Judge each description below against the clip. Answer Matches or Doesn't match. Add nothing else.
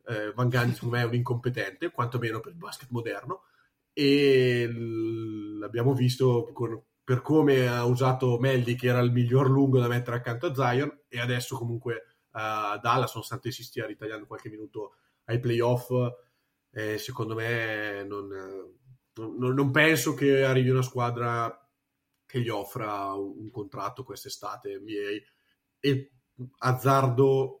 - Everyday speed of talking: Matches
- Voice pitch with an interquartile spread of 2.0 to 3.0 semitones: Matches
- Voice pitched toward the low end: Matches